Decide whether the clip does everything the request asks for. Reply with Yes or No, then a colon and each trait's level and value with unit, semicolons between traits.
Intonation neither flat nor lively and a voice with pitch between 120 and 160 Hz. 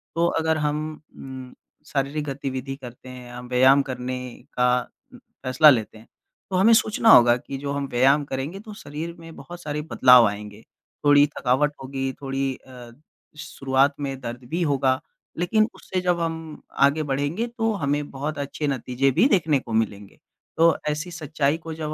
Yes: average, 3.5 semitones; medium, 140 Hz